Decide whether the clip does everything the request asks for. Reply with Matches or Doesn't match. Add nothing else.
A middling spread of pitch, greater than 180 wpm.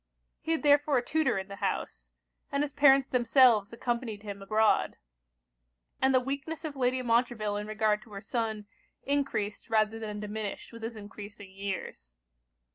Doesn't match